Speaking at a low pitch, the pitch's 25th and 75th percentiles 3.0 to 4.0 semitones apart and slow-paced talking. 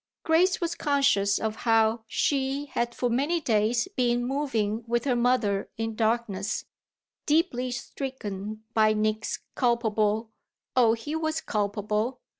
No: high, 235 Hz; average, 3.7 semitones; slow, 125 wpm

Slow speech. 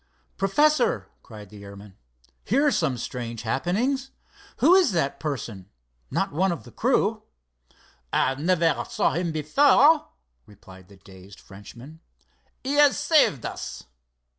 Yes: slow, 125 wpm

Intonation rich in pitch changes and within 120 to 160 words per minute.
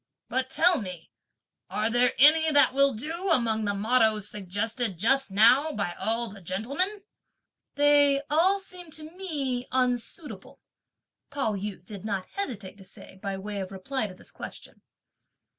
Yes: wide, 6.1 semitones; average, 150 wpm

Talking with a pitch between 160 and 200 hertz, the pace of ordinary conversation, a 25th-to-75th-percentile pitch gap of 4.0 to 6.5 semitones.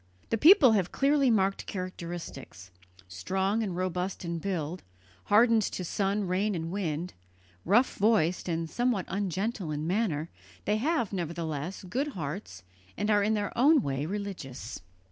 Yes: high, 190 Hz; average, 145 wpm; average, 4.3 semitones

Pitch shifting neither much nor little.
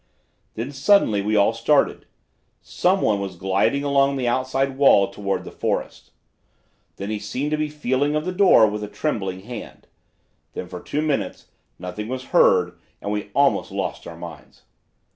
No: wide, 5.9 semitones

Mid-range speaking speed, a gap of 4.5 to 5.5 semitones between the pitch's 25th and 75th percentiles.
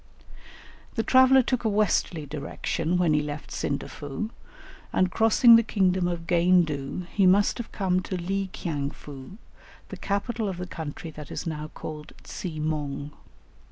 Yes: average, 155 wpm; average, 4.9 semitones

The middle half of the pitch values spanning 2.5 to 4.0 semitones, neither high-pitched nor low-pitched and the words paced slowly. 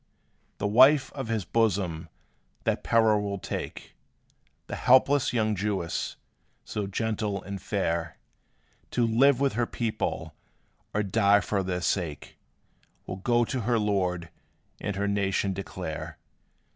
No: average, 3.3 semitones; low, 105 Hz; slow, 130 wpm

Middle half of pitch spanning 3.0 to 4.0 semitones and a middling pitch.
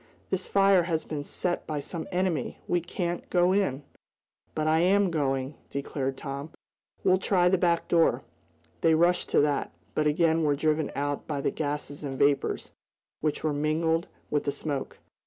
Yes: average, 3.4 semitones; medium, 155 Hz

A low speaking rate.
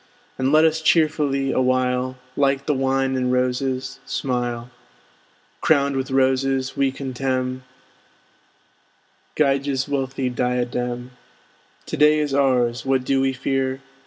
Yes: slow, 115 wpm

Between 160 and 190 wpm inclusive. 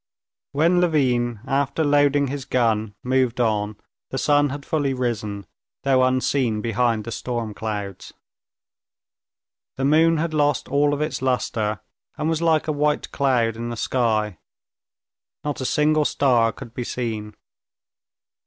No: average, 140 wpm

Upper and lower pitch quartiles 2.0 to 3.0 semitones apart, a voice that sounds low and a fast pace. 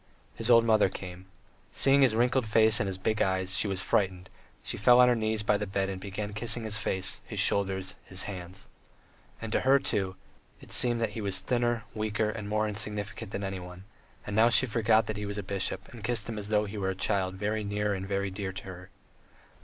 Yes: narrow, 2.4 semitones; low, 105 Hz; fast, 225 wpm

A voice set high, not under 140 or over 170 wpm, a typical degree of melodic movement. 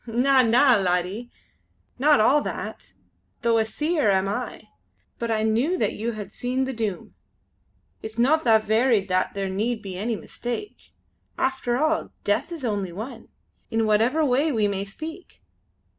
Yes: high, 230 Hz; average, 160 wpm; average, 4.1 semitones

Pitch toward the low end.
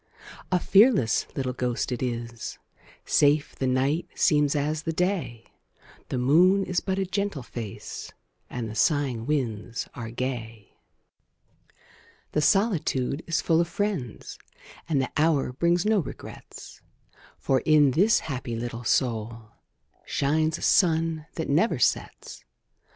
No: medium, 145 Hz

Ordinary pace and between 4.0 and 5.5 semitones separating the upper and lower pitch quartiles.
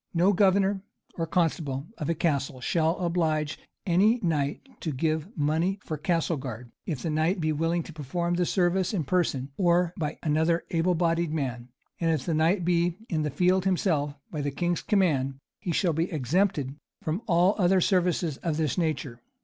No: average, 180 wpm; average, 2.9 semitones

